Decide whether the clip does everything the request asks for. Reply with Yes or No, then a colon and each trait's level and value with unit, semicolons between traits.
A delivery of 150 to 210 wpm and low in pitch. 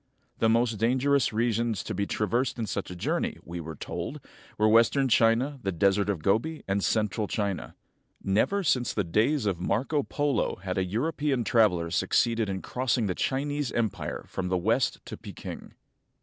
Yes: average, 170 wpm; low, 110 Hz